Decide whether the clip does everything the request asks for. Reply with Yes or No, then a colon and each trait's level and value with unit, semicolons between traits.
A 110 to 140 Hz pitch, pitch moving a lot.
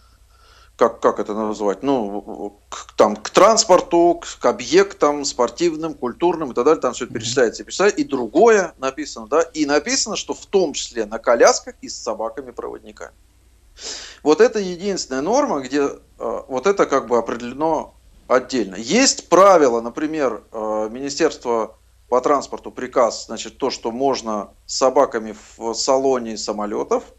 Yes: low, 135 Hz; wide, 6.7 semitones